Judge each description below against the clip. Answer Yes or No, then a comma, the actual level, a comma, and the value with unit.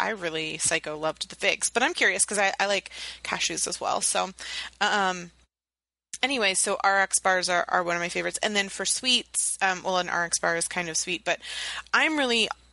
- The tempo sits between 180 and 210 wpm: Yes, fast, 205 wpm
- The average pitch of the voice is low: No, medium, 185 Hz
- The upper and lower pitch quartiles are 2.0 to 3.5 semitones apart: Yes, average, 3.2 semitones